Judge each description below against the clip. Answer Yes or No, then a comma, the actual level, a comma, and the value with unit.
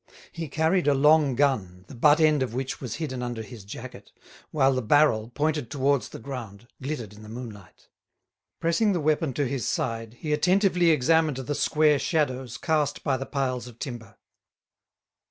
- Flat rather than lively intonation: No, average, 4.2 semitones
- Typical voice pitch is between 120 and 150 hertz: Yes, low, 135 Hz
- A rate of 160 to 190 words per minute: Yes, average, 170 wpm